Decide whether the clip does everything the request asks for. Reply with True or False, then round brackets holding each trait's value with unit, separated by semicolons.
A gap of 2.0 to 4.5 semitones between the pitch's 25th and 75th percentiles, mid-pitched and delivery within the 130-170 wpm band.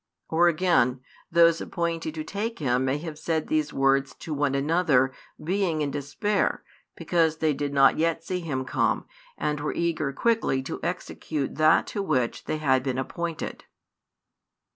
True (3.6 semitones; 155 Hz; 160 wpm)